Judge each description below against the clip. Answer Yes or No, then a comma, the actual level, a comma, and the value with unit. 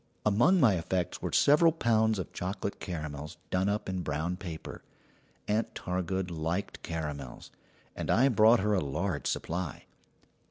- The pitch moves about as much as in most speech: Yes, average, 4.6 semitones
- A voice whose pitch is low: Yes, very low, 95 Hz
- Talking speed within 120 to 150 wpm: Yes, average, 145 wpm